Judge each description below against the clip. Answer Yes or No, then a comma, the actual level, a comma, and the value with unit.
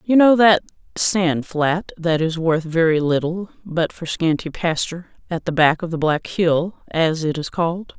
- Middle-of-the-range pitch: Yes, medium, 170 Hz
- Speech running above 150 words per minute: Yes, average, 190 wpm